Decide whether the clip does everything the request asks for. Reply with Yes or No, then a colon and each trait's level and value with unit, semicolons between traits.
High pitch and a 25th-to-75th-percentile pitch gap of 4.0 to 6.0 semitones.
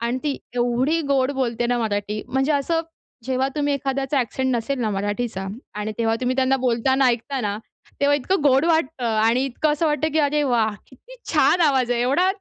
No: very high, 260 Hz; average, 3.2 semitones